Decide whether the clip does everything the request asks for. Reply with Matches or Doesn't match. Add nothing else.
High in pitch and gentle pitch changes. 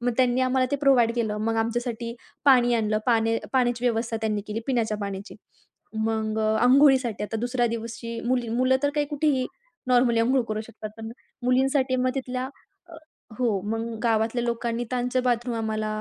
Matches